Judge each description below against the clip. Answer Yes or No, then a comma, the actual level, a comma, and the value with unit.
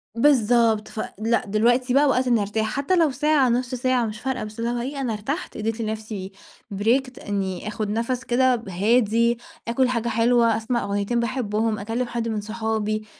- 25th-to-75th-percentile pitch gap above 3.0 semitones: No, average, 2.7 semitones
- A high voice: Yes, high, 230 Hz